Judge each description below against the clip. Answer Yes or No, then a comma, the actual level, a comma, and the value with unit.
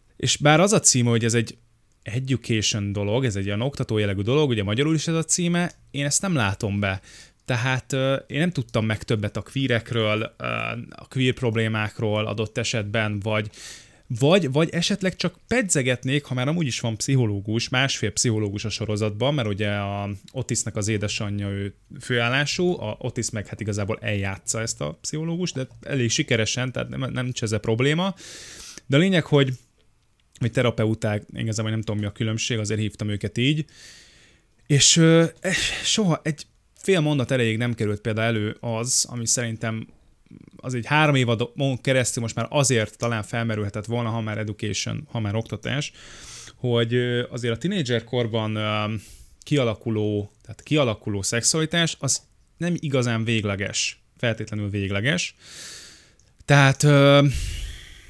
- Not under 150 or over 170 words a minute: Yes, fast, 155 wpm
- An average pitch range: Yes, average, 4.5 semitones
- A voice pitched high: No, low, 115 Hz